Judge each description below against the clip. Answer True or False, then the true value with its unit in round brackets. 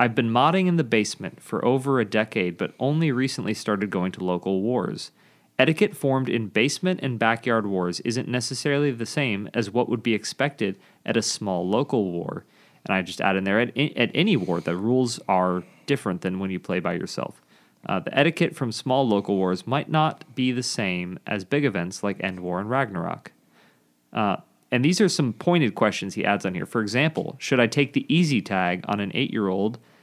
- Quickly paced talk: True (210 wpm)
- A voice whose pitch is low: True (120 Hz)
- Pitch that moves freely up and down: True (6.0 semitones)